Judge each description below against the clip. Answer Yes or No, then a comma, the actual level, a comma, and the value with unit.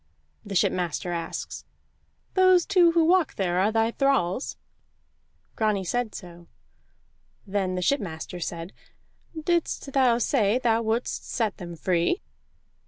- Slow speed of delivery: Yes, slow, 120 wpm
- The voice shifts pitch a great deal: Yes, wide, 7.3 semitones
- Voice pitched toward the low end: No, high, 215 Hz